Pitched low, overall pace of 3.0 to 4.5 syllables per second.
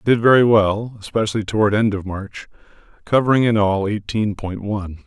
No: low, 105 Hz; 5.4 syllables/s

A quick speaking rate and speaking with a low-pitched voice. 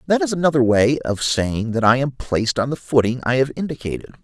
Yes: fast, 225 wpm; low, 130 Hz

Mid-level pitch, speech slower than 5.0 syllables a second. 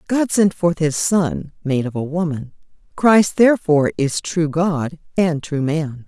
Yes: medium, 165 Hz; 4.1 syllables/s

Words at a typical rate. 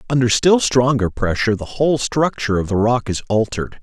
Yes: average, 190 wpm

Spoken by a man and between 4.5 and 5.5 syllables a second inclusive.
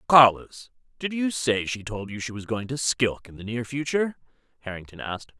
Yes: male; 5.4 syllables/s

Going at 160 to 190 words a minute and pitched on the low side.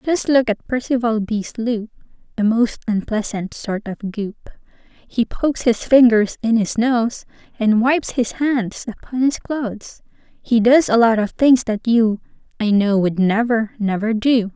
No: average, 165 wpm; high, 230 Hz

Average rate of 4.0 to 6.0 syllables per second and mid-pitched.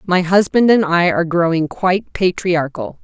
Yes: 4.8 syllables/s; medium, 180 Hz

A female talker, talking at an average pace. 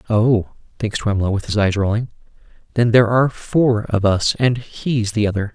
No: male; average, 185 wpm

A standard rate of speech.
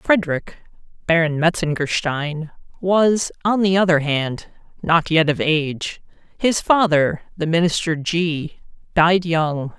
No: slow, 115 wpm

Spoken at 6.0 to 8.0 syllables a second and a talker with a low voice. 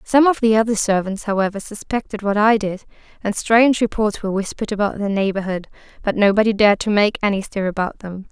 No: 6.2 syllables/s; high, 205 Hz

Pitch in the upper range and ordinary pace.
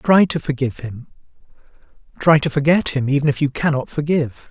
No: medium, 145 Hz; average, 175 wpm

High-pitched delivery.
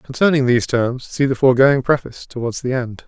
No: low, 130 Hz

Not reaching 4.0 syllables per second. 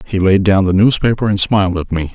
No: 6.0 syllables/s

